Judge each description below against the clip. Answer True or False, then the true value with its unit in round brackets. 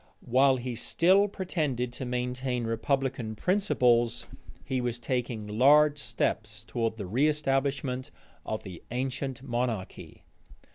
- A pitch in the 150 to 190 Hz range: False (125 Hz)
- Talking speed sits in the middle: False (110 wpm)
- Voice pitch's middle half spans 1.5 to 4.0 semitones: True (2.9 semitones)